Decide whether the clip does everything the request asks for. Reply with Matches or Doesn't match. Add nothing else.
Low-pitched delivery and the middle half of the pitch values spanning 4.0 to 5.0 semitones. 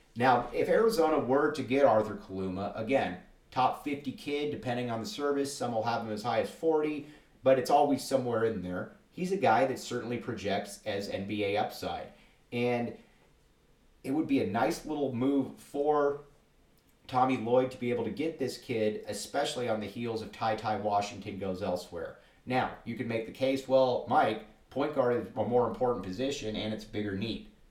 Matches